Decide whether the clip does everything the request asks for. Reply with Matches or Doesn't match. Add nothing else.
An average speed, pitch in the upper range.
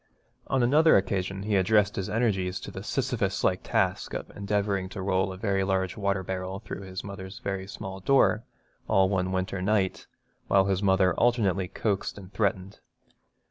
Doesn't match